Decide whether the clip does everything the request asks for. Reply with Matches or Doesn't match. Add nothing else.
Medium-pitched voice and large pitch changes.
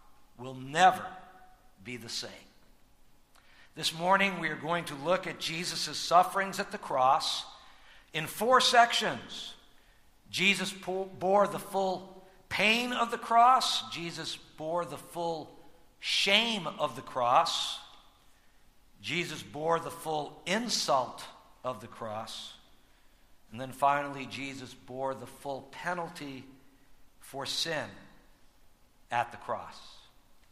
Matches